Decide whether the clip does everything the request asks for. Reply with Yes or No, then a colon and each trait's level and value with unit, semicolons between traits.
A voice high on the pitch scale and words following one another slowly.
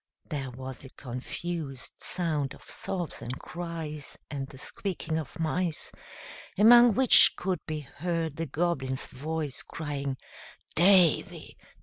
No: medium, 155 Hz; slow, 120 wpm